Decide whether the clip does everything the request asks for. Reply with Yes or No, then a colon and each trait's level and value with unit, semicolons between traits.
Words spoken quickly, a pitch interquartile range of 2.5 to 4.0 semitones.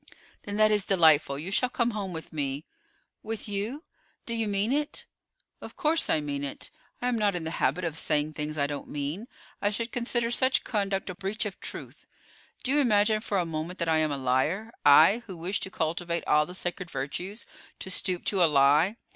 No: fast, 210 wpm; wide, 5.6 semitones